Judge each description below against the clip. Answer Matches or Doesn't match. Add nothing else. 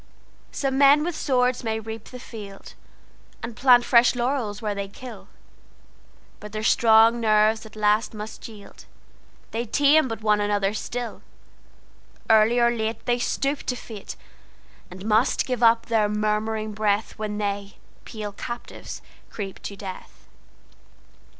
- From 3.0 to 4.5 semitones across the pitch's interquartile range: Doesn't match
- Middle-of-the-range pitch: Doesn't match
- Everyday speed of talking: Doesn't match